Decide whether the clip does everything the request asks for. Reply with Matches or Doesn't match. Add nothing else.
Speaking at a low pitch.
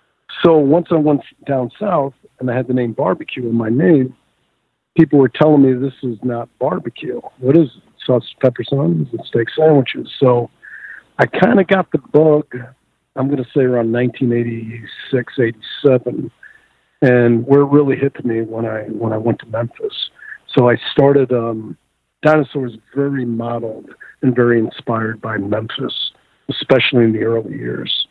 Matches